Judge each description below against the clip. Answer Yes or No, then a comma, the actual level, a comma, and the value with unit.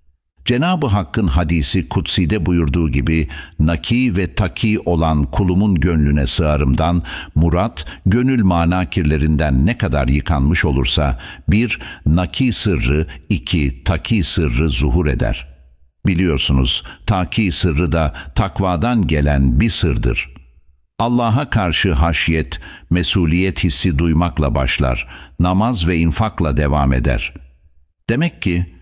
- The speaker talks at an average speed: Yes, average, 105 wpm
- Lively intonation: No, average, 4.3 semitones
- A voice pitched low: Yes, very low, 85 Hz